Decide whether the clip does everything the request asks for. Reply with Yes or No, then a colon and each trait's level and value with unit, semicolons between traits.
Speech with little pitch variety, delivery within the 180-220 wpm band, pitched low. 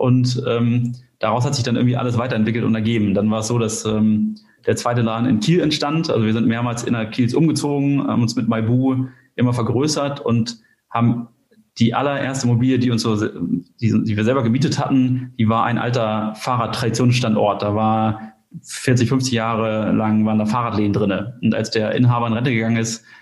Yes: narrow, 2.3 semitones; average, 185 wpm; low, 120 Hz